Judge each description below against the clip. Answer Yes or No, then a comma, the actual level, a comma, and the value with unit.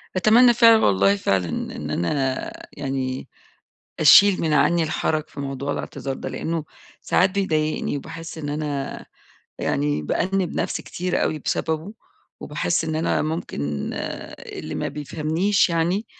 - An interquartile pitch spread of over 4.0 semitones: Yes, average, 4.5 semitones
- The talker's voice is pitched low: No, medium, 155 Hz